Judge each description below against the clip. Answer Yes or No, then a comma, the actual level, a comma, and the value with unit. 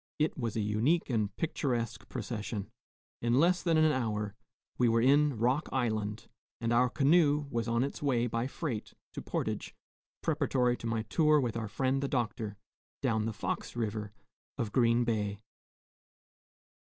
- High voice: No, low, 120 Hz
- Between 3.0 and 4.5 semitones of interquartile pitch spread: Yes, average, 3.8 semitones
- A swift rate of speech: No, average, 155 wpm